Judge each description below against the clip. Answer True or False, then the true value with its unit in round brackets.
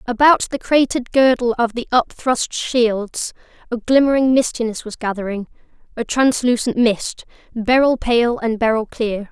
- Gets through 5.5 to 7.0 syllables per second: False (4.5 syllables/s)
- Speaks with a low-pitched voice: False (240 Hz)